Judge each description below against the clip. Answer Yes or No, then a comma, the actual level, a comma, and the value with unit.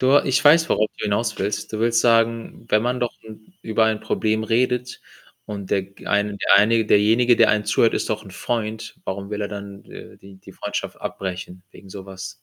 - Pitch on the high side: No, low, 110 Hz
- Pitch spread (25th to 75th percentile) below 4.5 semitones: Yes, narrow, 2.5 semitones